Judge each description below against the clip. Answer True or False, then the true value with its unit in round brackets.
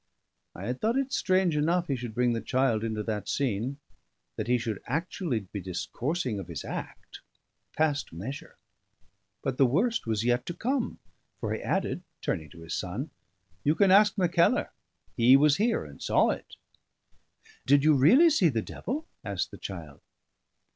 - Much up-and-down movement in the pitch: True (8.0 semitones)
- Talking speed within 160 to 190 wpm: True (170 wpm)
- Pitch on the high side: False (135 Hz)